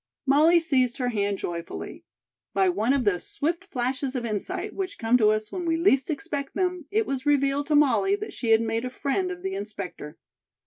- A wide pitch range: Yes, wide, 6.9 semitones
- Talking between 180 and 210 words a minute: Yes, fast, 205 wpm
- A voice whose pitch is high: Yes, very high, 275 Hz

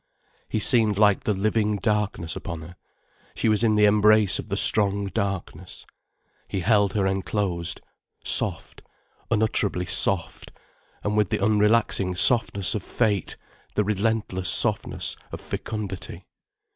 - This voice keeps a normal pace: No, slow, 130 wpm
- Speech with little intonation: Yes, narrow, 1.9 semitones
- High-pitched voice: No, low, 105 Hz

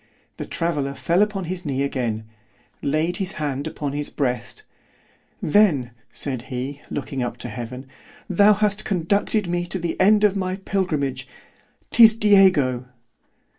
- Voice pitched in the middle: Yes, medium, 155 Hz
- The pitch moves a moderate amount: No, wide, 6.8 semitones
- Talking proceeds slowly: Yes, slow, 130 wpm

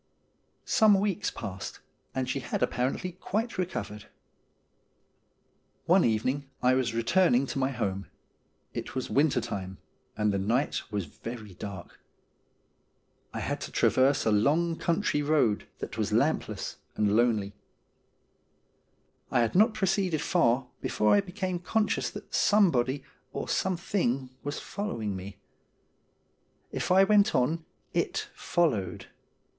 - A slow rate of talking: Yes, slow, 125 wpm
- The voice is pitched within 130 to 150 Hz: Yes, low, 135 Hz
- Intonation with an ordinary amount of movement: No, wide, 8.6 semitones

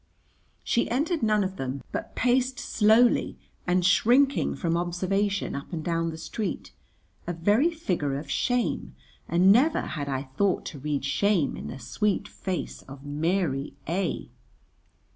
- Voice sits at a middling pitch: Yes, medium, 180 Hz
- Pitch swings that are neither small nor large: No, wide, 6.3 semitones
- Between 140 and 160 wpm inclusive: Yes, average, 145 wpm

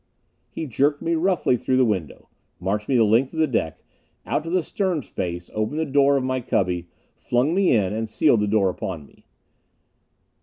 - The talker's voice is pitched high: No, low, 125 Hz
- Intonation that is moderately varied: No, wide, 6.6 semitones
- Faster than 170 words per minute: Yes, average, 195 wpm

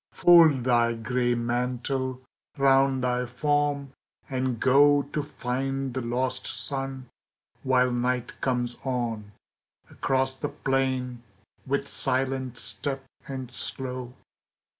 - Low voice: Yes, low, 130 Hz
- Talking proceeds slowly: Yes, slow, 105 wpm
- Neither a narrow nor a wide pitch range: No, narrow, 1.5 semitones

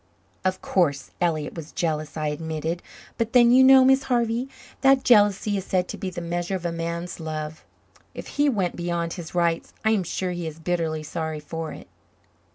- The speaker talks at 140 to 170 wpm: No, average, 190 wpm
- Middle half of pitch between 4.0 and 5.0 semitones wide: Yes, average, 4.3 semitones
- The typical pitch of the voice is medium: Yes, medium, 175 Hz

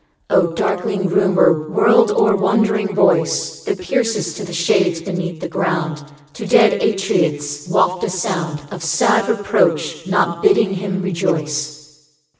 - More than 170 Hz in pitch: Yes, medium, 185 Hz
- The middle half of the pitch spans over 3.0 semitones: Yes, average, 4.2 semitones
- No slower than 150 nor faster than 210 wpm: No, slow, 135 wpm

